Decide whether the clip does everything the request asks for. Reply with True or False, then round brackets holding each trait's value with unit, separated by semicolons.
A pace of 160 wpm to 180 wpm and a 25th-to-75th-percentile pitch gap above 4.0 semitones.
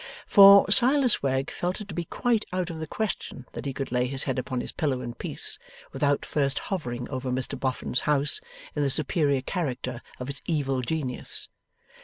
False (190 wpm; 5.1 semitones)